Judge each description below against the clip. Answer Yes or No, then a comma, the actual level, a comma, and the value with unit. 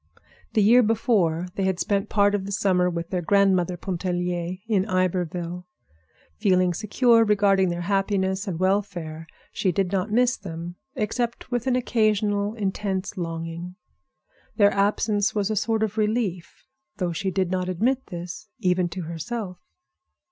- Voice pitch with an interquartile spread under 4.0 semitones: Yes, average, 2.9 semitones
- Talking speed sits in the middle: Yes, average, 150 wpm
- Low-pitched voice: No, high, 190 Hz